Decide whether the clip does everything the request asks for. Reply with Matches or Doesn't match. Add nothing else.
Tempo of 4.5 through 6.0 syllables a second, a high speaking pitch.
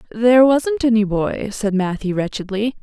Matches